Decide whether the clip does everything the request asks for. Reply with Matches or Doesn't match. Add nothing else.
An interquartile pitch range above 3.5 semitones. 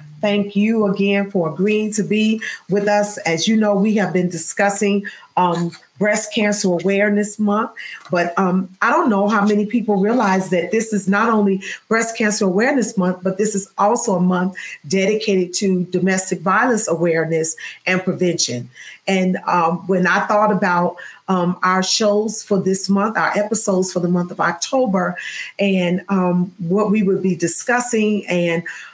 Doesn't match